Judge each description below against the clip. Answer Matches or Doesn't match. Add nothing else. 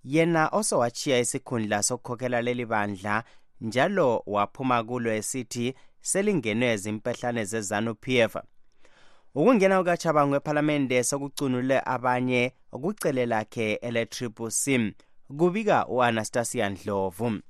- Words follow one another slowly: Matches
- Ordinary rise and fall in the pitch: Matches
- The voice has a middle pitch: Doesn't match